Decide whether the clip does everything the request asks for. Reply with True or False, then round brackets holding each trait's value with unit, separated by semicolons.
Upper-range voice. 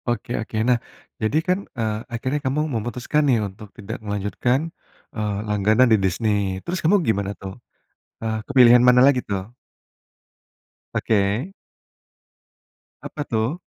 False (115 Hz)